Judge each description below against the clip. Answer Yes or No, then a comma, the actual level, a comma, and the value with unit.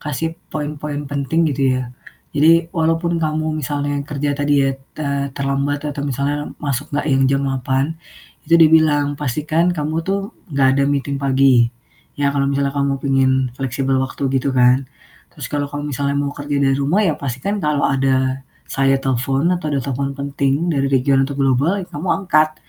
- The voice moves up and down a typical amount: No, narrow, 2.1 semitones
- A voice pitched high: No, medium, 140 Hz